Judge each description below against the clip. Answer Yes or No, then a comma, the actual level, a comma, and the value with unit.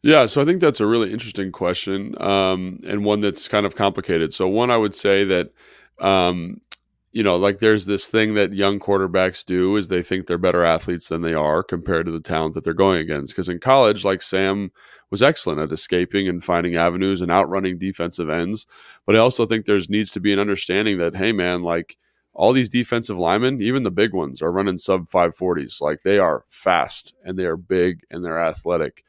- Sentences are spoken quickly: Yes, fast, 210 wpm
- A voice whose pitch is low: Yes, very low, 95 Hz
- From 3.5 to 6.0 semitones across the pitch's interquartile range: No, average, 2.8 semitones